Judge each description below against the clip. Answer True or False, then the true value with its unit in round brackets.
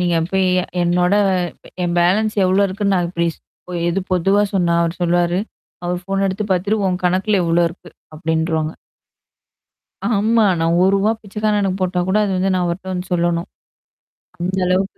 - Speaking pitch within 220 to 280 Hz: False (185 Hz)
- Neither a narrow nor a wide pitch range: False (2.1 semitones)